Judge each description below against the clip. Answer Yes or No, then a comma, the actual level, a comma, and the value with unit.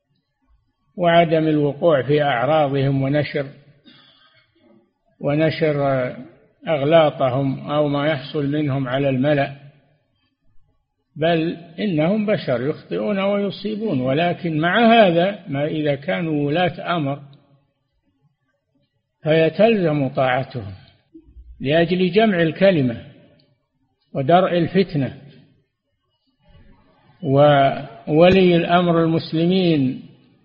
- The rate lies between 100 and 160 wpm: No, average, 70 wpm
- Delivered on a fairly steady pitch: No, average, 3.8 semitones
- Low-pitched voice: No, medium, 145 Hz